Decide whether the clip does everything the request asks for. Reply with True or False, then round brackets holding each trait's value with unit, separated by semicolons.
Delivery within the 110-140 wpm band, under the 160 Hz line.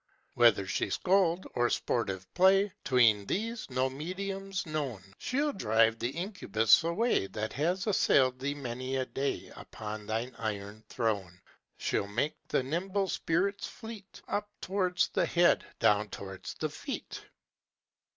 True (135 wpm; 135 Hz)